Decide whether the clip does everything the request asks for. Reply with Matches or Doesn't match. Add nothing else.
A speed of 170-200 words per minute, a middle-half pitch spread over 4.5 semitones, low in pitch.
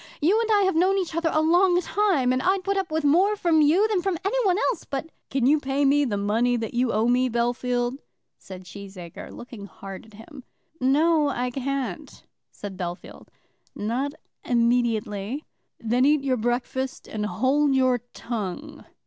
Doesn't match